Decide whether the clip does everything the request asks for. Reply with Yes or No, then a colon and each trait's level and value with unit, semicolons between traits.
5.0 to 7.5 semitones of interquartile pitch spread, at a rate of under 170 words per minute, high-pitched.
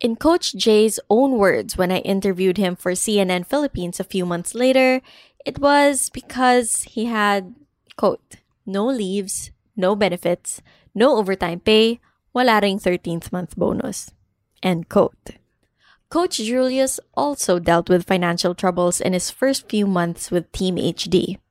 Yes: wide, 5.5 semitones; average, 140 wpm; high, 195 Hz